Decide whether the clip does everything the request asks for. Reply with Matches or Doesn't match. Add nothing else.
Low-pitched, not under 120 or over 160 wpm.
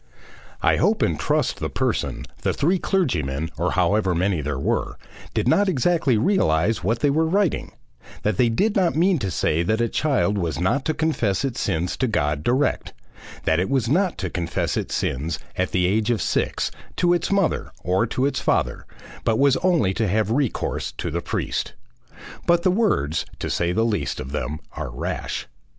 Doesn't match